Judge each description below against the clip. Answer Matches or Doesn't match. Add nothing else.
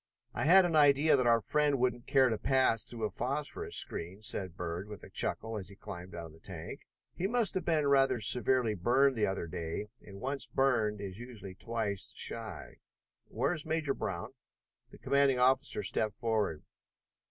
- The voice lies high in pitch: Doesn't match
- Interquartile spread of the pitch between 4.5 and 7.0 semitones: Matches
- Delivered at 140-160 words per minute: Doesn't match